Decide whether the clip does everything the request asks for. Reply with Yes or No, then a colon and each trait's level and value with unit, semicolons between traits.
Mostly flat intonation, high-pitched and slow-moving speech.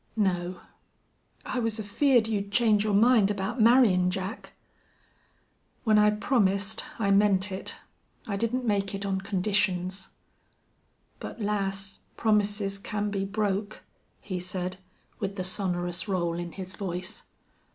Yes: narrow, 2.1 semitones; high, 200 Hz; slow, 130 wpm